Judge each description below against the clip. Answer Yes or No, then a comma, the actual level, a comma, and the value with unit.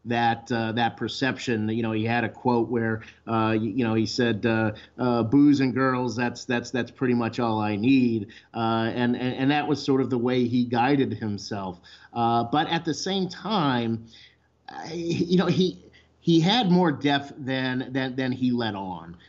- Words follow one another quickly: No, average, 195 wpm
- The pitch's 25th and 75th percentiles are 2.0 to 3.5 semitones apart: Yes, average, 3.1 semitones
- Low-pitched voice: Yes, low, 120 Hz